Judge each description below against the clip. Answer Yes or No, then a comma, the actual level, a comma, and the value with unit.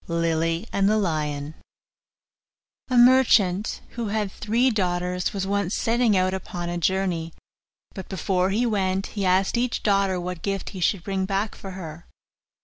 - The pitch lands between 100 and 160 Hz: No, high, 190 Hz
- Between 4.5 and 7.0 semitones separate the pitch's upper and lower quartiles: No, average, 2.8 semitones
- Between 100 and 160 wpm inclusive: Yes, average, 155 wpm